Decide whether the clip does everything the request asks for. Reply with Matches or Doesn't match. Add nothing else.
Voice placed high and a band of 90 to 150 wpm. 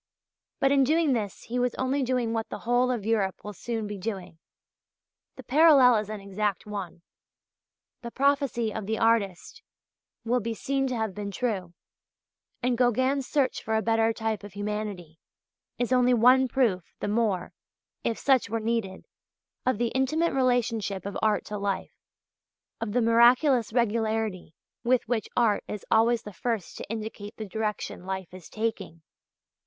Doesn't match